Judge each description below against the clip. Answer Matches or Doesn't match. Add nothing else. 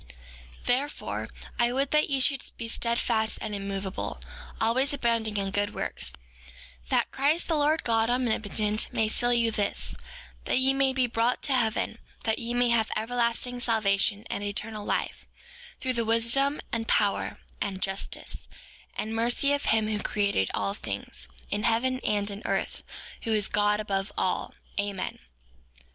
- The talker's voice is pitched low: Doesn't match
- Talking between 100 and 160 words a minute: Matches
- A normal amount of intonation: Matches